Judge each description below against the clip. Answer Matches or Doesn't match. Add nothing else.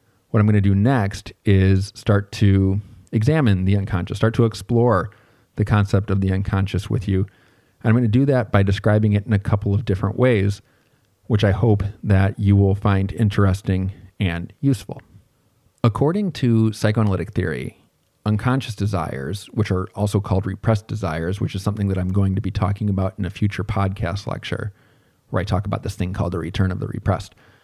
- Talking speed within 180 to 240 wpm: Matches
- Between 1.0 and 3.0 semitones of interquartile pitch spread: Matches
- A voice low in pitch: Matches